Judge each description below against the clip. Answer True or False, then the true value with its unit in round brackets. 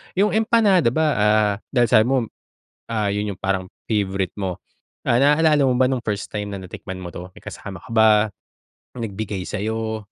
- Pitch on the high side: False (110 Hz)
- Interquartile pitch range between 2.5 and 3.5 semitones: False (4.4 semitones)